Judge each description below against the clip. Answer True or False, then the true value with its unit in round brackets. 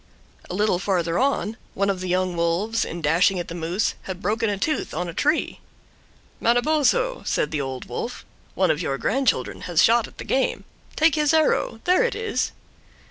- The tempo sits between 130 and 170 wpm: False (190 wpm)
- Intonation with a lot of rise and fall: True (8.0 semitones)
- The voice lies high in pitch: True (200 Hz)